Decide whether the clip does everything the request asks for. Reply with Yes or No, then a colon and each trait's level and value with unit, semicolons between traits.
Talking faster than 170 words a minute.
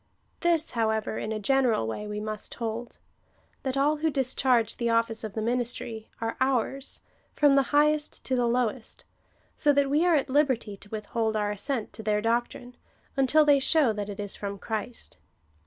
Yes: average, 185 wpm